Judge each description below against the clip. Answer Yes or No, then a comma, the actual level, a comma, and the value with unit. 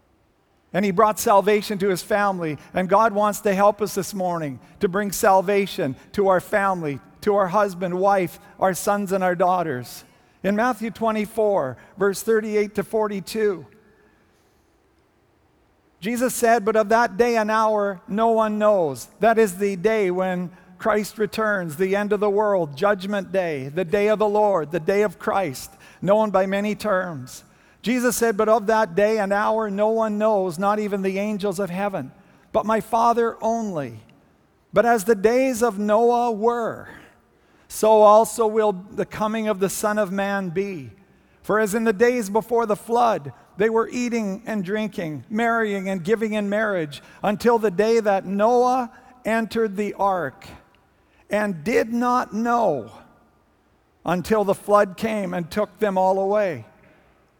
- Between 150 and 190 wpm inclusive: Yes, average, 160 wpm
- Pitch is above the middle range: Yes, high, 210 Hz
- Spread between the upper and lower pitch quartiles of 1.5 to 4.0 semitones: Yes, narrow, 2.4 semitones